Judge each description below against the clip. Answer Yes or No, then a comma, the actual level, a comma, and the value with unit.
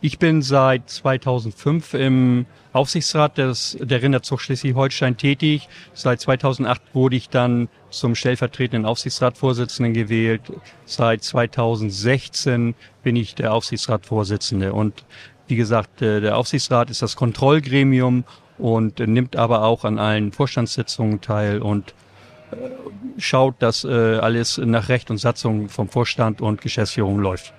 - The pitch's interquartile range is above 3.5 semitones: No, average, 3.0 semitones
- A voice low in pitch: Yes, low, 125 Hz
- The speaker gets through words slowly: Yes, slow, 120 wpm